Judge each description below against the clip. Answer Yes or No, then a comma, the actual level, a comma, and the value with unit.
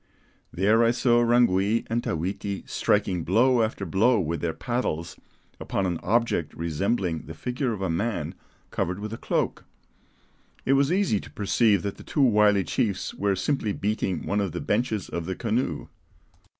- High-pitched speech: No, low, 105 Hz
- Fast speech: No, average, 165 wpm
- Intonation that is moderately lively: Yes, average, 4.5 semitones